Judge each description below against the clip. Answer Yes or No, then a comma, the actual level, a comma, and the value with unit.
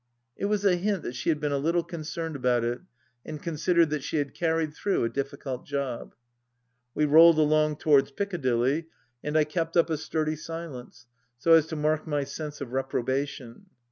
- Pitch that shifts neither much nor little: Yes, average, 3.0 semitones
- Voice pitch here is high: No, medium, 150 Hz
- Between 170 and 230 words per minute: Yes, average, 180 wpm